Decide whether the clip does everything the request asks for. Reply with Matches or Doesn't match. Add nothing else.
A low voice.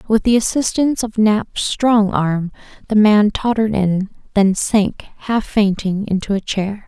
Doesn't match